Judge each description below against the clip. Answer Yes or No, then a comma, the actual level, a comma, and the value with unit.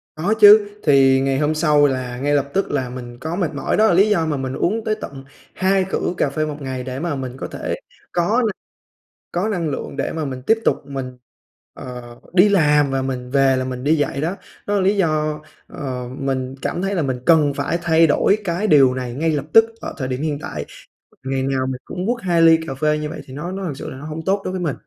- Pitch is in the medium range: Yes, medium, 150 Hz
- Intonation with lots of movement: No, average, 4.7 semitones